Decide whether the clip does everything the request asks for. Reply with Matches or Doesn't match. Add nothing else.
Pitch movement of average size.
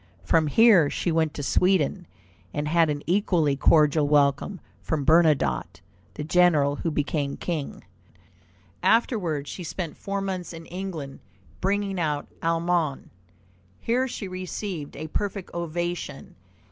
Matches